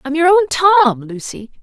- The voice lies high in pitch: Yes, very high, 305 Hz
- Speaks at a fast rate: No, average, 185 wpm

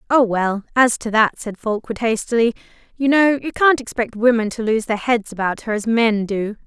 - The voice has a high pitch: Yes, high, 230 Hz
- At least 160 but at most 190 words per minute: No, fast, 205 wpm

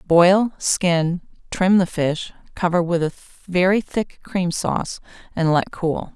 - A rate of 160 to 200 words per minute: No, slow, 135 wpm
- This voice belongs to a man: No, female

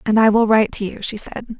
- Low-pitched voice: No, high, 215 Hz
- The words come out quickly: Yes, fast, 300 wpm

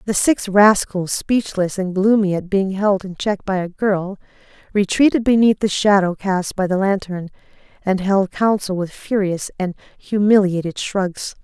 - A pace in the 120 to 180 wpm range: Yes, average, 155 wpm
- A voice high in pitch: Yes, high, 195 Hz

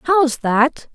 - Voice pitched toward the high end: Yes, very high, 275 Hz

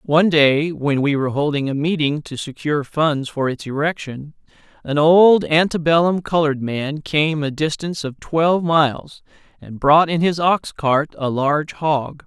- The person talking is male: Yes, male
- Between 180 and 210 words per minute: No, average, 170 wpm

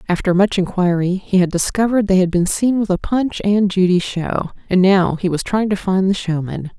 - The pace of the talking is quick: Yes, fast, 220 wpm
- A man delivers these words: No, female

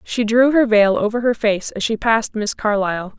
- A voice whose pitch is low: No, high, 220 Hz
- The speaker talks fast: Yes, fast, 225 wpm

